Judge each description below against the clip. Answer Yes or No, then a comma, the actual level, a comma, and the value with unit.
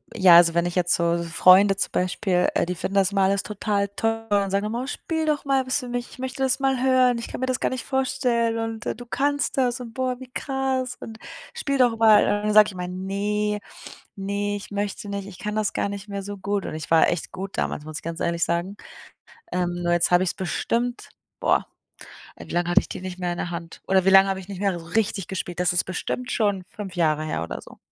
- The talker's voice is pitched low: No, high, 200 Hz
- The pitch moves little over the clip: No, average, 4.9 semitones